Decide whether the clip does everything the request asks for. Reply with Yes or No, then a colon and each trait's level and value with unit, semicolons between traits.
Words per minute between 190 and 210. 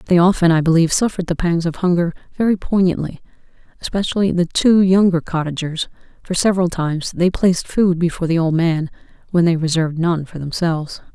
No: average, 170 wpm